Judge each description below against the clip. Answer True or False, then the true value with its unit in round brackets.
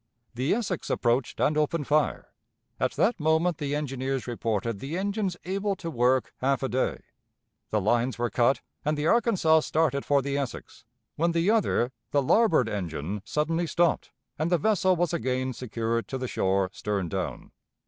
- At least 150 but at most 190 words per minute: True (170 wpm)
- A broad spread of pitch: True (5.7 semitones)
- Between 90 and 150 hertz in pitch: True (140 Hz)